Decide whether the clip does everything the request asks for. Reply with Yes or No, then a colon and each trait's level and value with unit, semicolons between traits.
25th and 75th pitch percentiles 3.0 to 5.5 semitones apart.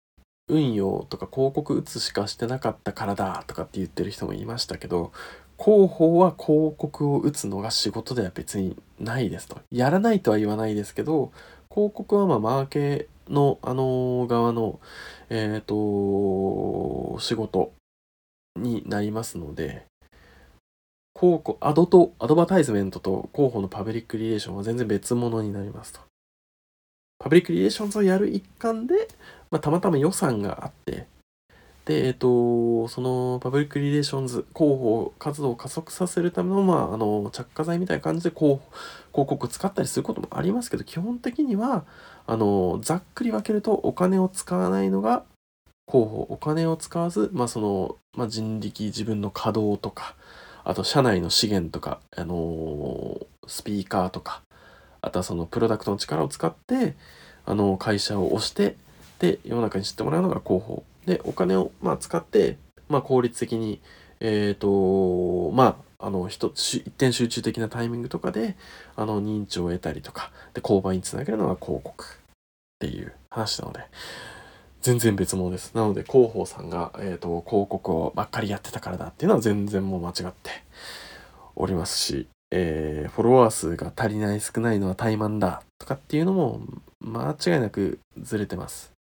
No: wide, 7.2 semitones